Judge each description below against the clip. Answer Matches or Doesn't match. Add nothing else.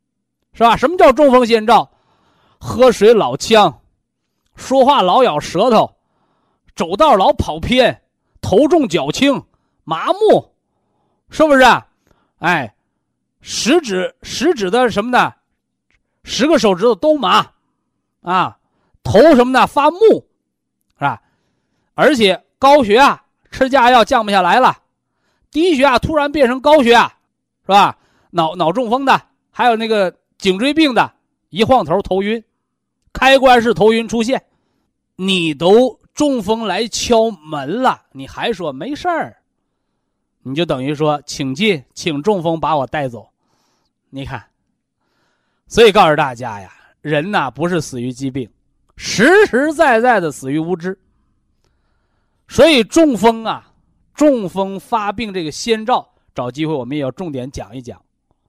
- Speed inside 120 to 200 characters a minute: Matches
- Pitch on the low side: Doesn't match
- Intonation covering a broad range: Matches